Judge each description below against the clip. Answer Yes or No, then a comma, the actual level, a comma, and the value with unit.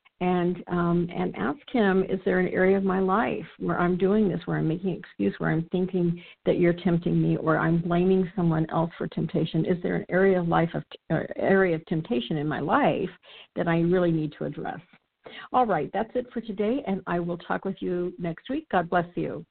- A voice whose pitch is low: No, medium, 180 Hz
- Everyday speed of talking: No, fast, 220 wpm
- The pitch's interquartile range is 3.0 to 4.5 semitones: No, narrow, 2.4 semitones